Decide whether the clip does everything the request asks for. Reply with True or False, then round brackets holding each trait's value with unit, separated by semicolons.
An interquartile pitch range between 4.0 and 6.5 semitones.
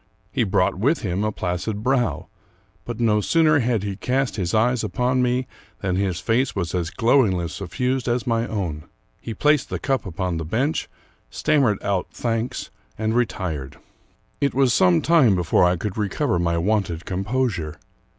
True (5.6 semitones)